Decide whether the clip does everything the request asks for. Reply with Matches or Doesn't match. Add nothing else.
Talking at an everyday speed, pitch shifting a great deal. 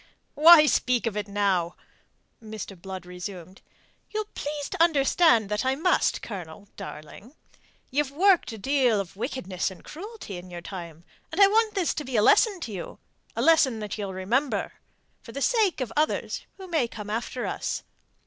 Matches